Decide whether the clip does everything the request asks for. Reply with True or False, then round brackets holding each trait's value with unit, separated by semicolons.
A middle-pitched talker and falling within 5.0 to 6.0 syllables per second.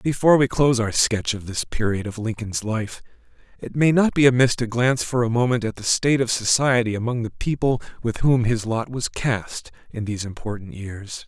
False (120 Hz; 5.4 syllables/s)